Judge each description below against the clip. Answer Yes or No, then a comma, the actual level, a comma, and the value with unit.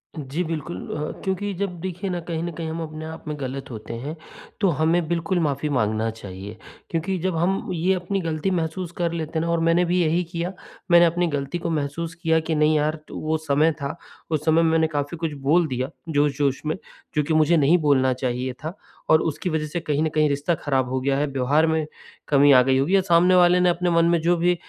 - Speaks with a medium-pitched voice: Yes, medium, 160 Hz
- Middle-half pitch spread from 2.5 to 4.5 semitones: Yes, average, 3.1 semitones